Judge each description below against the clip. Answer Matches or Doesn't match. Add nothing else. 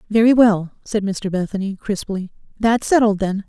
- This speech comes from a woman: Matches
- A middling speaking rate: Matches